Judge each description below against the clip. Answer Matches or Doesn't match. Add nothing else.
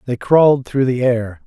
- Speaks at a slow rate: Doesn't match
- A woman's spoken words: Doesn't match